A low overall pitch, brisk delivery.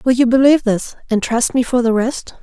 No: high, 245 Hz; fast, 225 wpm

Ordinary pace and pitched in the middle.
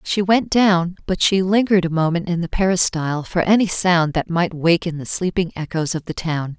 No: fast, 210 wpm; medium, 175 Hz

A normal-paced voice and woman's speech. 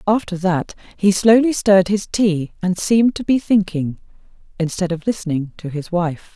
Yes: average, 170 wpm; female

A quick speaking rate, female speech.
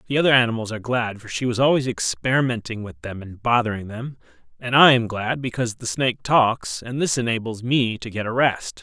No: fast, 210 wpm; male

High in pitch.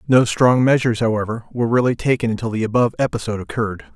No: low, 115 Hz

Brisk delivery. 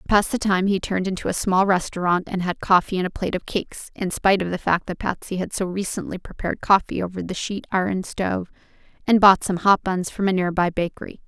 Yes: fast, 240 wpm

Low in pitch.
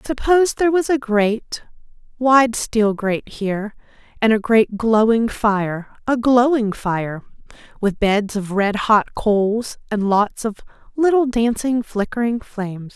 No: high, 225 Hz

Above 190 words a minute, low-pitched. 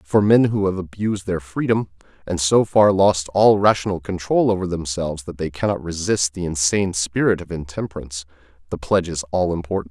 No: average, 180 wpm; very low, 90 Hz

